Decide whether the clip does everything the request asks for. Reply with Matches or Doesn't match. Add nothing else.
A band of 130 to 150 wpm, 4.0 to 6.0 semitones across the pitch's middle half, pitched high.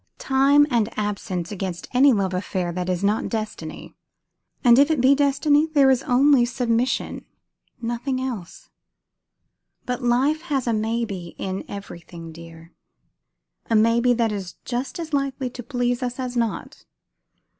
Matches